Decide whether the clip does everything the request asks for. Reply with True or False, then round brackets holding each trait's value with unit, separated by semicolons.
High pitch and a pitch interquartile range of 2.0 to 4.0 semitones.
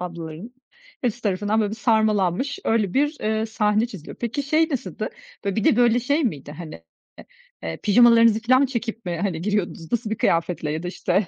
False (215 Hz; 5.0 semitones)